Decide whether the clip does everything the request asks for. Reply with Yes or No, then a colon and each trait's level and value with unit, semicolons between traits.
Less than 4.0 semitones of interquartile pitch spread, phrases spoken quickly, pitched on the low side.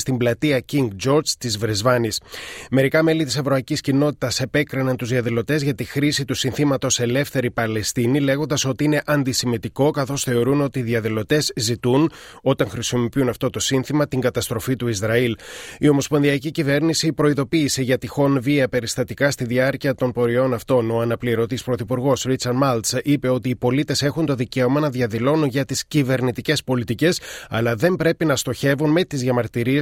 No: average, 2.8 semitones; average, 160 wpm; low, 130 Hz